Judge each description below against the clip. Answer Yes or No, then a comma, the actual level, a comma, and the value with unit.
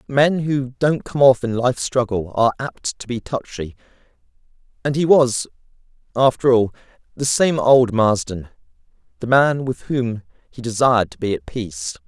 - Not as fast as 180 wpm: Yes, average, 160 wpm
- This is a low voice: Yes, low, 120 Hz